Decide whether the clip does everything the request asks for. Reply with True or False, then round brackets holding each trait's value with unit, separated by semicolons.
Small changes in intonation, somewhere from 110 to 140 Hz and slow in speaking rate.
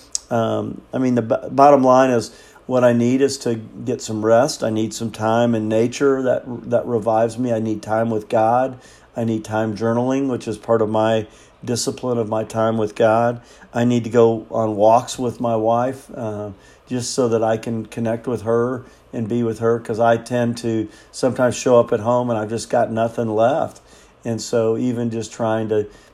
False (1.6 semitones; 115 Hz; 205 wpm)